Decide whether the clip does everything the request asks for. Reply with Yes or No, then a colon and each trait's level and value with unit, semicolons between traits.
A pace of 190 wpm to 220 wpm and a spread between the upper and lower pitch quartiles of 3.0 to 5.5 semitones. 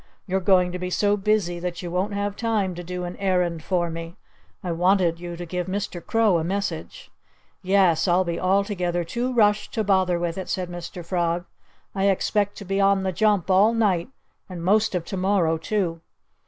No: average, 195 wpm; narrow, 2.6 semitones